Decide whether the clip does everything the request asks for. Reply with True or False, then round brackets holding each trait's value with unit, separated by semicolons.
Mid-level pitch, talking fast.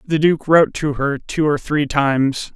True (145 Hz; 210 wpm)